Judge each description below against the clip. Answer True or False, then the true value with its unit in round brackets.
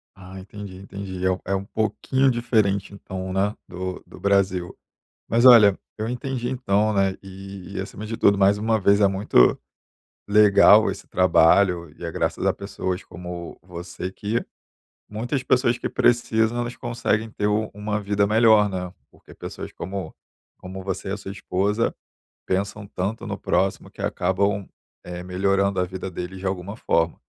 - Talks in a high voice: False (100 Hz)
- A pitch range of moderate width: False (2.3 semitones)